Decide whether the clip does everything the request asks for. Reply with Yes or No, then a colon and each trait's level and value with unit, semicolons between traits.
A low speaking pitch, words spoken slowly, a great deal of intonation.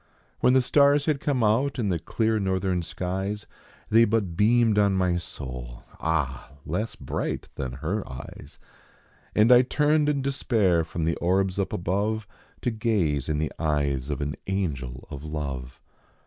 No: very low, 95 Hz; average, 160 wpm; wide, 6.7 semitones